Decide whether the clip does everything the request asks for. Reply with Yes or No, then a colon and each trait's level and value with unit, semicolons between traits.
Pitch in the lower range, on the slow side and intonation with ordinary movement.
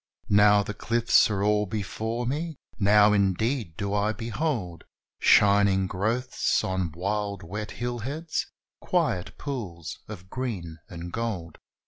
Yes: low, 105 Hz; slow, 120 wpm; average, 3.7 semitones